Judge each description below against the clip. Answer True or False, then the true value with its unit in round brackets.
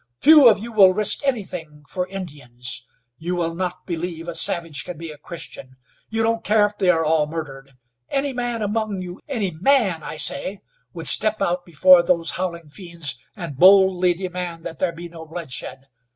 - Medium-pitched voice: True (175 Hz)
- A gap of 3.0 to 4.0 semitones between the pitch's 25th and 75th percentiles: True (3.4 semitones)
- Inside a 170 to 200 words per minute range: True (180 wpm)